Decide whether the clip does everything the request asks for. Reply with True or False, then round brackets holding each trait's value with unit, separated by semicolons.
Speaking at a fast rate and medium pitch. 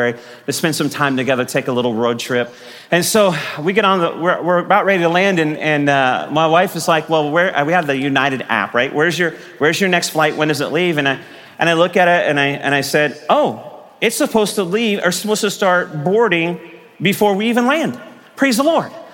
True (240 wpm; 165 Hz)